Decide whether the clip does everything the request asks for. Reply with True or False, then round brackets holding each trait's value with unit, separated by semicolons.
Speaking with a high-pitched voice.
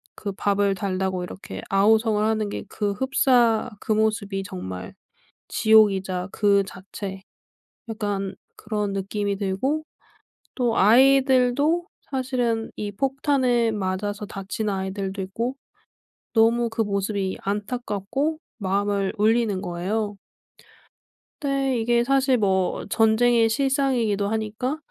True (215 Hz)